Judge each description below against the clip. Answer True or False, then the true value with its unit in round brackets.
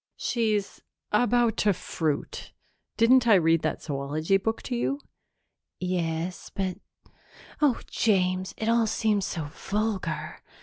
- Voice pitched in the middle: False (195 Hz)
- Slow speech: True (120 wpm)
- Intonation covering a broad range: False (4.3 semitones)